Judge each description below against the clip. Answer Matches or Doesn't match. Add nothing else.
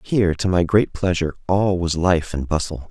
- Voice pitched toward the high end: Doesn't match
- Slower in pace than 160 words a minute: Doesn't match